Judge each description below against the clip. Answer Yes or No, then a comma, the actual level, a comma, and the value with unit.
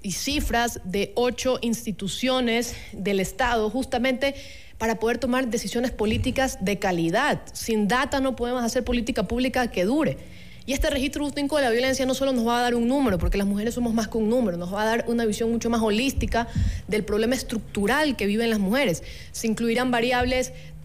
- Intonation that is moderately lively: Yes, average, 3.1 semitones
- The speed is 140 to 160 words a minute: No, fast, 190 wpm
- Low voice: No, high, 235 Hz